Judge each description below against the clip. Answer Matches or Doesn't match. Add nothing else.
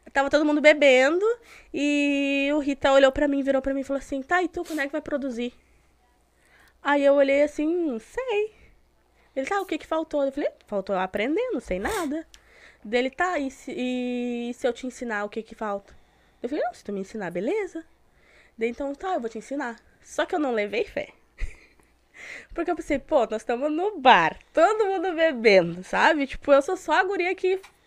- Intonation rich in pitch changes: Doesn't match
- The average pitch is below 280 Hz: Doesn't match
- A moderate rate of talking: Doesn't match